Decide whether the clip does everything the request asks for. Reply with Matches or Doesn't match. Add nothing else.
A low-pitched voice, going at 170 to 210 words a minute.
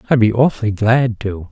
Matches